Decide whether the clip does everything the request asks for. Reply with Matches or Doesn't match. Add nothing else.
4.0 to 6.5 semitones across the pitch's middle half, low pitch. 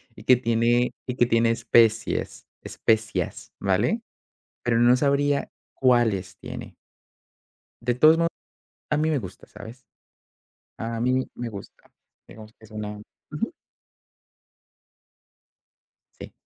Doesn't match